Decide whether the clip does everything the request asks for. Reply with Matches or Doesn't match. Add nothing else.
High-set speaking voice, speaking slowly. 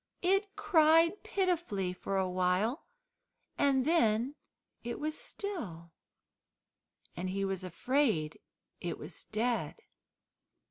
Matches